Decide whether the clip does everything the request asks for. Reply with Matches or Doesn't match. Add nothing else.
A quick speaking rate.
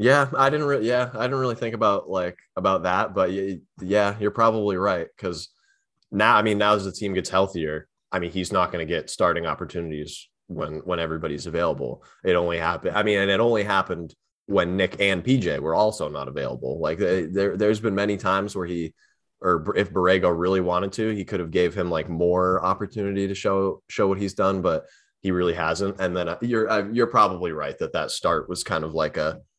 Matches